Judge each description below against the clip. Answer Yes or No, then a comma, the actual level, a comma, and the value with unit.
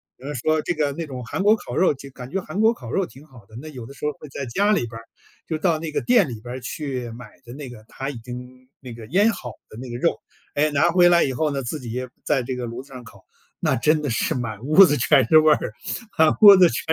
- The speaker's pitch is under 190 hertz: Yes, low, 135 Hz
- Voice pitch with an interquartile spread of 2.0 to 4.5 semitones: Yes, average, 4.2 semitones